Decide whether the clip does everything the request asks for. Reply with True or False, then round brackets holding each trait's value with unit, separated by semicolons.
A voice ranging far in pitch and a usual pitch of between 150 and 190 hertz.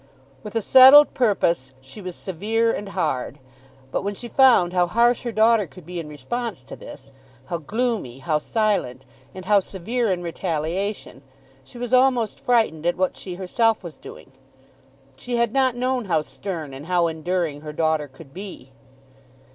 True (6.3 semitones; 185 Hz)